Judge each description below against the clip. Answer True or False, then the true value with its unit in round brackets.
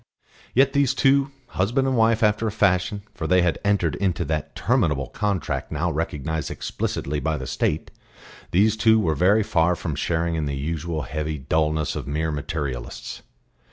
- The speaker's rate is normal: True (165 wpm)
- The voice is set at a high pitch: False (85 Hz)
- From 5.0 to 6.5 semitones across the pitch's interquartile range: True (5.3 semitones)